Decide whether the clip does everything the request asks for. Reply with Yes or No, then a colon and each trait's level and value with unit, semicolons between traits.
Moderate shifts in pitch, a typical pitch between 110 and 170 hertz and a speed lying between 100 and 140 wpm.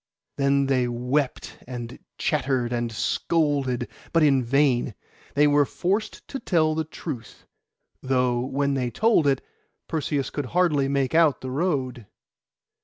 Yes: average, 3.3 semitones; medium, 140 Hz; slow, 135 wpm